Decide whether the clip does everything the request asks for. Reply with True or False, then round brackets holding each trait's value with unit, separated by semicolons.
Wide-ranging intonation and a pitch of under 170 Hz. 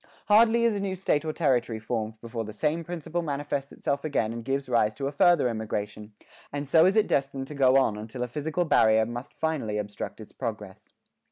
True (6.1 semitones; 135 Hz)